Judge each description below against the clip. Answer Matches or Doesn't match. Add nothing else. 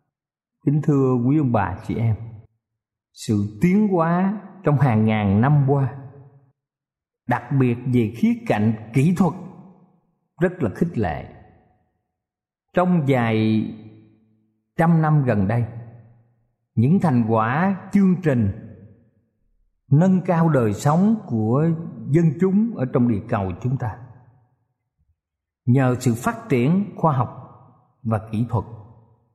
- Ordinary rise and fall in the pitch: Doesn't match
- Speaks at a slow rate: Matches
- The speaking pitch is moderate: Doesn't match